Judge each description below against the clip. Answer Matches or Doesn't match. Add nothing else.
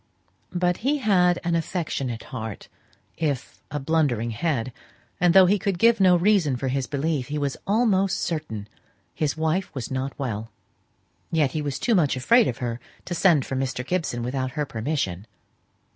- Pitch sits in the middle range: Matches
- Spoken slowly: Doesn't match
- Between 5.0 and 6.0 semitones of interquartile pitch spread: Matches